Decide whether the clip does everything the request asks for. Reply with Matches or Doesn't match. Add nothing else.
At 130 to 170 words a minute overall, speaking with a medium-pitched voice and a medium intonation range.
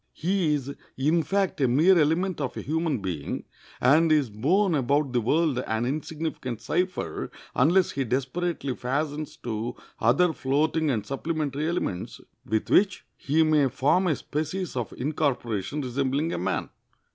Matches